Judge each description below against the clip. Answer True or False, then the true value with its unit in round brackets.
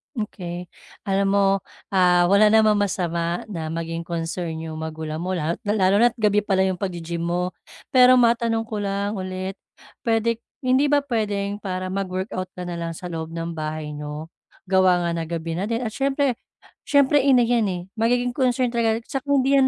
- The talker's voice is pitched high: True (195 Hz)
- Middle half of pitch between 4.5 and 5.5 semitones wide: True (5.1 semitones)